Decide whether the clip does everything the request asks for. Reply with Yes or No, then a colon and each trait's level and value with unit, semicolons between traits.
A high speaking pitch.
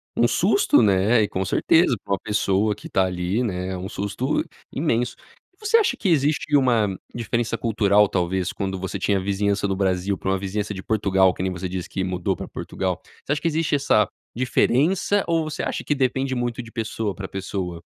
No: low, 105 Hz